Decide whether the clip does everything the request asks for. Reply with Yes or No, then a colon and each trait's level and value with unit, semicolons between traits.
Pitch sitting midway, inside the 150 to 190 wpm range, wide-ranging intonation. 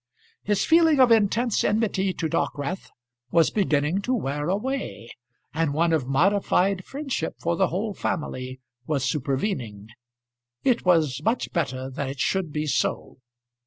No: medium, 170 Hz; average, 140 wpm; wide, 6.5 semitones